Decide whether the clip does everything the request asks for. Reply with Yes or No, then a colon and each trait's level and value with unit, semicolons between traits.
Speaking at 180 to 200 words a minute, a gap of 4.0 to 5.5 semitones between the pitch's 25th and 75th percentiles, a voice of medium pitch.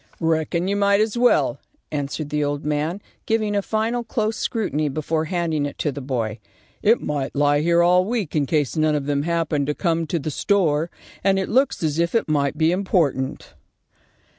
Yes: average, 190 wpm; average, 5.1 semitones; medium, 160 Hz